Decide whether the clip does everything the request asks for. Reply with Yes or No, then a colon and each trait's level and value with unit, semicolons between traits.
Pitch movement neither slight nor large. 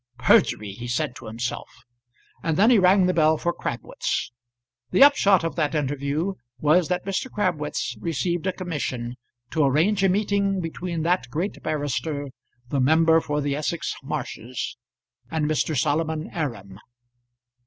Yes: average, 4.3 semitones